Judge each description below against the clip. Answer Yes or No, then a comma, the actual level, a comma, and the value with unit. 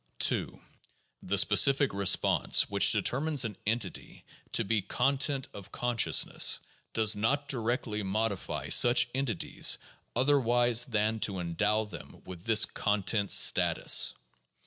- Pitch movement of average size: Yes, average, 3.5 semitones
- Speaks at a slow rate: Yes, slow, 115 wpm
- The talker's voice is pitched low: Yes, low, 110 Hz